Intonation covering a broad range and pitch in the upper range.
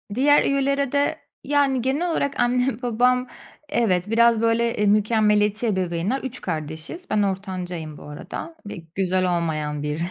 Yes: wide, 6.1 semitones; high, 220 Hz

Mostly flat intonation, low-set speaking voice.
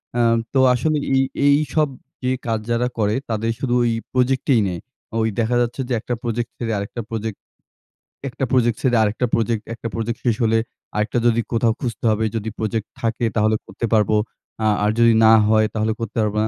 Yes: narrow, 1.9 semitones; low, 115 Hz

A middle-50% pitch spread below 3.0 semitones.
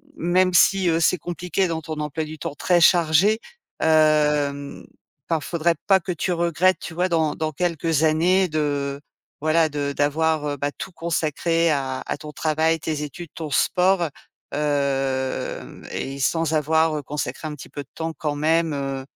Yes: narrow, 2.5 semitones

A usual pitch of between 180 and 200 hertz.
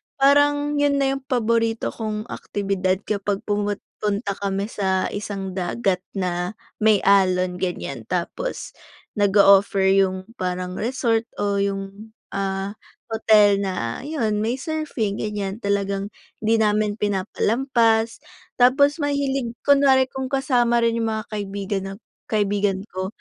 No: high, 210 Hz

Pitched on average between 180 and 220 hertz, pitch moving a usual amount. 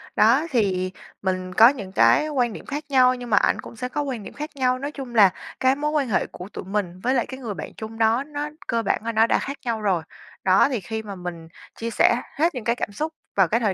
No: high, 230 Hz; average, 4.9 semitones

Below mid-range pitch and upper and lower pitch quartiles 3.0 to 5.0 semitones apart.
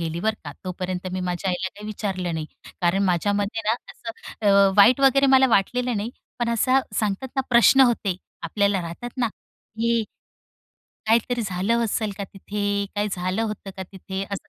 No: high, 205 Hz; average, 3.8 semitones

